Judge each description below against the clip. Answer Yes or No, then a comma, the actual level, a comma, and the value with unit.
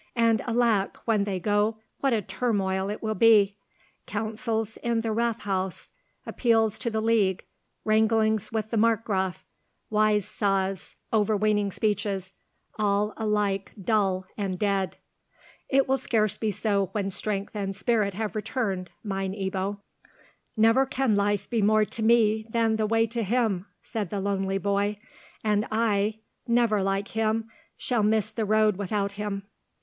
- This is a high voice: Yes, high, 210 Hz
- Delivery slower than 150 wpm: Yes, average, 140 wpm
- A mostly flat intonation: Yes, narrow, 2.0 semitones